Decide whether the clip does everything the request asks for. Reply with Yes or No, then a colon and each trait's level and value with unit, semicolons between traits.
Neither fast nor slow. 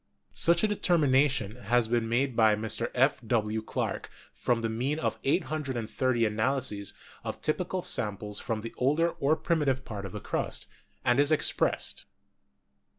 Yes: average, 155 wpm